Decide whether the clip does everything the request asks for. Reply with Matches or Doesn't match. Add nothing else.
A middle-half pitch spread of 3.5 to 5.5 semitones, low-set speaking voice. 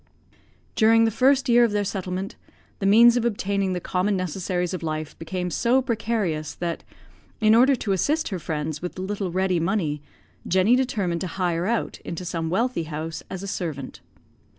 Doesn't match